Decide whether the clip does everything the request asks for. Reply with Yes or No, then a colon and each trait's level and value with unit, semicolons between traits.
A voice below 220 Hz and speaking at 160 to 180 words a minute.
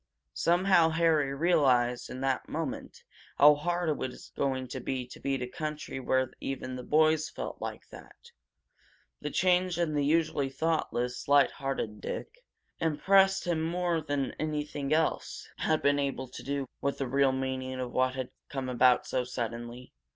Yes: medium, 140 Hz; average, 165 wpm